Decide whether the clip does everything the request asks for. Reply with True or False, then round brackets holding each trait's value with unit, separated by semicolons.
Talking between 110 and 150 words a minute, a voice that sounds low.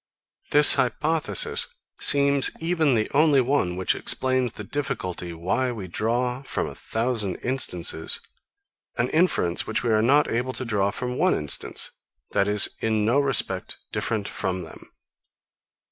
True (145 wpm; 120 Hz)